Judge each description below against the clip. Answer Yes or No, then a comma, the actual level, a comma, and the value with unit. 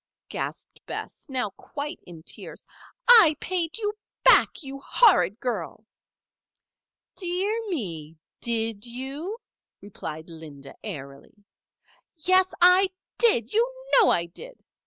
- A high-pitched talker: Yes, very high, 265 Hz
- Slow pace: Yes, slow, 110 wpm